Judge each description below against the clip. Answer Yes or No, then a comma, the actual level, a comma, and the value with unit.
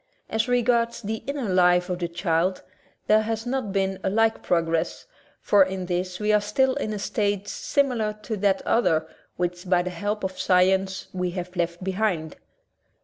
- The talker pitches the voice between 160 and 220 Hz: Yes, high, 190 Hz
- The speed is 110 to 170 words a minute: No, average, 180 wpm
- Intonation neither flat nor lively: Yes, average, 3.4 semitones